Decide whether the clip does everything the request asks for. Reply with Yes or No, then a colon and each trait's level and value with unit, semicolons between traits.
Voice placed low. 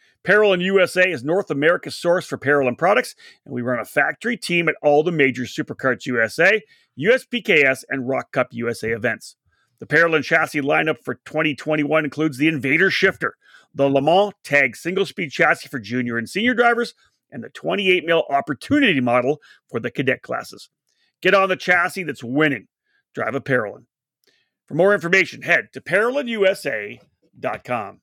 No: medium, 160 Hz